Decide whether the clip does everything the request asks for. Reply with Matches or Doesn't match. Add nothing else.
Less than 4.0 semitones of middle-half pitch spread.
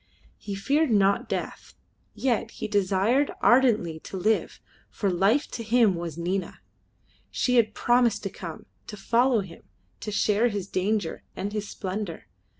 Matches